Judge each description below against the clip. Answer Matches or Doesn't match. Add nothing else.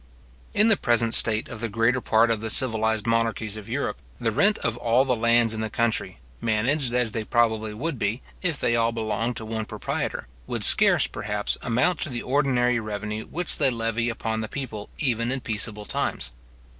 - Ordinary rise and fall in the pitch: Doesn't match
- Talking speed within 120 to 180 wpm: Doesn't match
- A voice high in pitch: Doesn't match